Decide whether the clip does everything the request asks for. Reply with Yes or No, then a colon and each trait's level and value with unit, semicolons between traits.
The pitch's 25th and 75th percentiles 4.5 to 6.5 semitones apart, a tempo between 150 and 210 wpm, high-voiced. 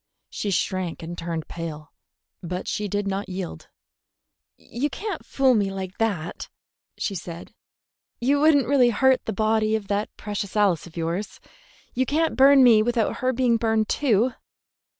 Yes: average, 5.3 semitones; average, 160 wpm; high, 215 Hz